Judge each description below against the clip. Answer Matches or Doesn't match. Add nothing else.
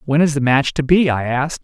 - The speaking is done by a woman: Doesn't match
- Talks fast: Matches